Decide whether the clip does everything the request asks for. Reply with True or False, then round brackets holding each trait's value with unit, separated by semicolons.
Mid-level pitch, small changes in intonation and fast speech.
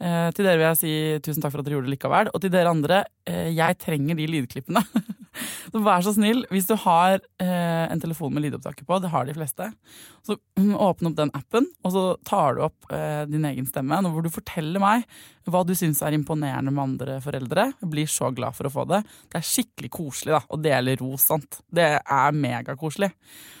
False (165 Hz; 4.3 semitones; 210 wpm)